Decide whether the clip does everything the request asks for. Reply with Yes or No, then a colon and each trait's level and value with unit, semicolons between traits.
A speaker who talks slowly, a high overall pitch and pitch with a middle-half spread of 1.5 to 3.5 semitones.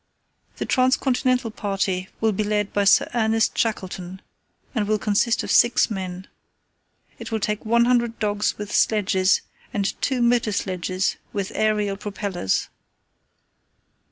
Yes: slow, 130 wpm; high, 210 Hz; average, 2.7 semitones